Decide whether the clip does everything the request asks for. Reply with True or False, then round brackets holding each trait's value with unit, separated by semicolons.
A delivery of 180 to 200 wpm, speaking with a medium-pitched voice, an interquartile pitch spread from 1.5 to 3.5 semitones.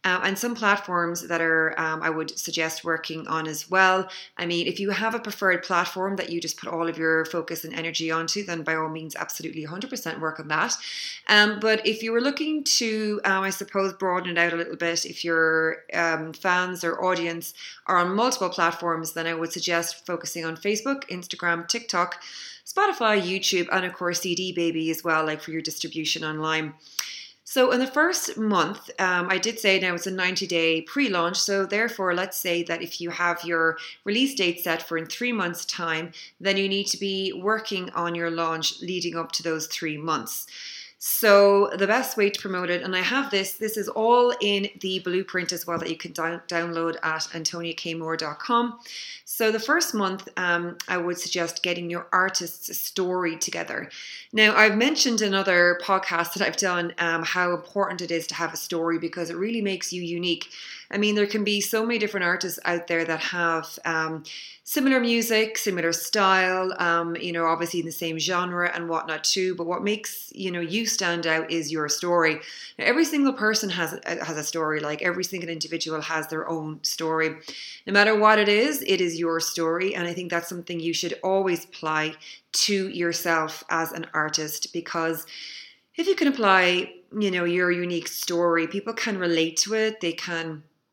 True (195 wpm; 175 Hz; 3.1 semitones)